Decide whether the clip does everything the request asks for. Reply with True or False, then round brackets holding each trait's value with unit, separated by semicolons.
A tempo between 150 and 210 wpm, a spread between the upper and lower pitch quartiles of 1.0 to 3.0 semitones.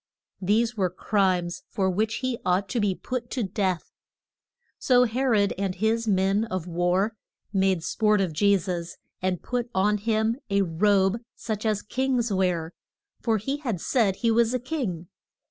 False (165 wpm; 3.6 semitones)